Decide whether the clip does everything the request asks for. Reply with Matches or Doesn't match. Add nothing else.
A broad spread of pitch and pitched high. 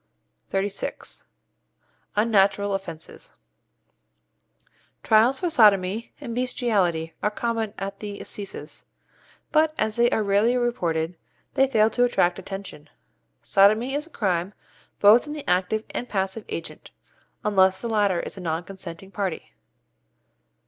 Doesn't match